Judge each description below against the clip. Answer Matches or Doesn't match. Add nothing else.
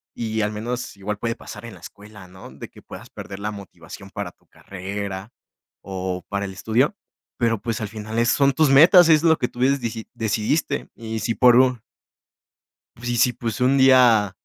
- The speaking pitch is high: Doesn't match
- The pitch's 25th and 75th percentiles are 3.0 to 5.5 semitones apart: Matches